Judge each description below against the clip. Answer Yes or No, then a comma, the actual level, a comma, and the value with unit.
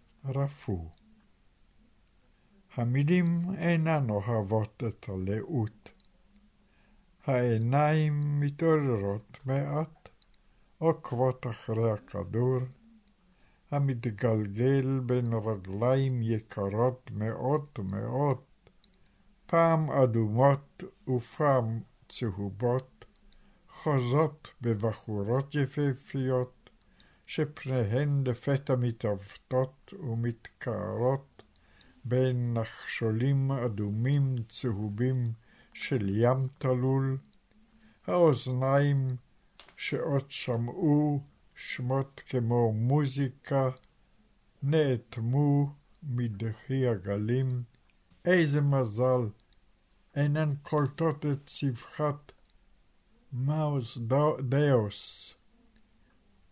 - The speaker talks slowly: Yes, slow, 55 wpm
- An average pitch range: Yes, average, 4.0 semitones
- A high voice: No, low, 130 Hz